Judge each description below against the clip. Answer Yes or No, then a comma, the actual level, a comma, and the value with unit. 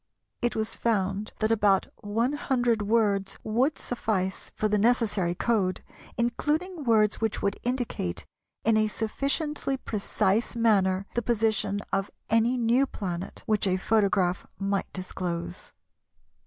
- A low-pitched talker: No, high, 215 Hz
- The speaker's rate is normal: No, slow, 130 wpm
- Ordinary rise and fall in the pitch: Yes, average, 3.3 semitones